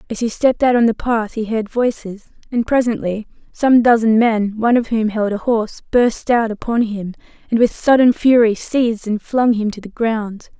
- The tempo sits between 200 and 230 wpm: Yes, fast, 205 wpm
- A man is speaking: No, female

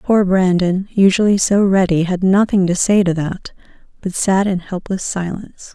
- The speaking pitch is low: No, high, 190 Hz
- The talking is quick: No, average, 165 wpm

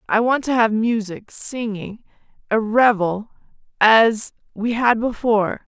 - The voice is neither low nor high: No, high, 225 Hz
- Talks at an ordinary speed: No, slow, 125 wpm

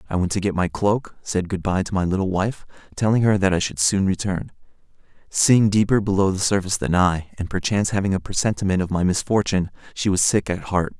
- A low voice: Yes, very low, 95 Hz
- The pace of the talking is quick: Yes, fast, 220 wpm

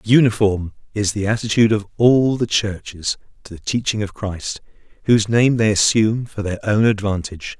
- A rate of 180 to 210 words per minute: No, average, 165 wpm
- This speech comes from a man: Yes, male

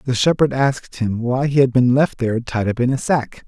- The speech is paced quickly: Yes, fast, 260 wpm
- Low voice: Yes, low, 125 Hz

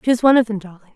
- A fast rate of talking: Yes, fast, 315 wpm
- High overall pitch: Yes, high, 220 Hz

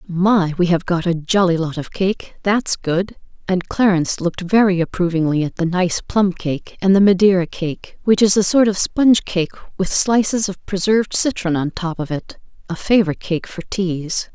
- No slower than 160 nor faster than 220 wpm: Yes, average, 190 wpm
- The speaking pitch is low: No, medium, 185 Hz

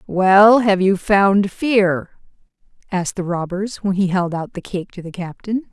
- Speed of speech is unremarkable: Yes, average, 180 wpm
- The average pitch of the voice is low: No, high, 190 Hz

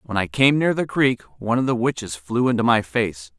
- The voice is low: Yes, low, 115 Hz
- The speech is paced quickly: Yes, fast, 250 wpm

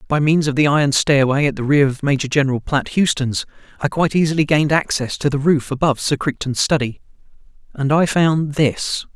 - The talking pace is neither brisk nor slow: Yes, average, 190 wpm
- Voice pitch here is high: No, medium, 145 Hz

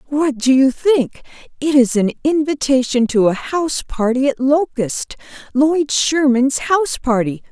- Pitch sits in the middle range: No, very high, 270 Hz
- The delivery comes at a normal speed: Yes, average, 145 wpm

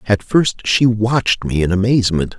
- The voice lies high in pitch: No, low, 105 Hz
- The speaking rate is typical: Yes, average, 175 wpm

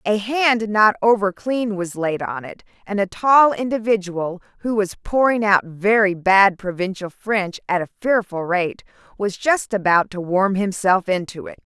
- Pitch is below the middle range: No, high, 200 Hz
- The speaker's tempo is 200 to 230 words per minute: No, average, 170 wpm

